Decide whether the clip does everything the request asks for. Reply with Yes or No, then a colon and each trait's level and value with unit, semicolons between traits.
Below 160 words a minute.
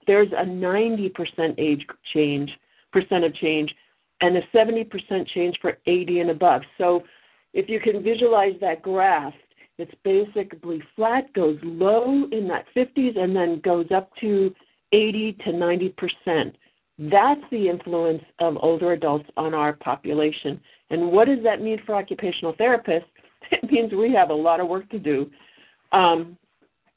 Yes: average, 145 wpm